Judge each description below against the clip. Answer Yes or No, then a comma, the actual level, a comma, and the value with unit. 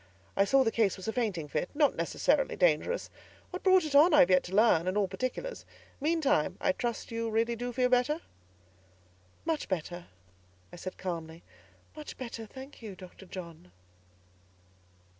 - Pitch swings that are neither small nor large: No, wide, 7.4 semitones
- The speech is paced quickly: No, average, 170 wpm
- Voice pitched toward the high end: Yes, high, 230 Hz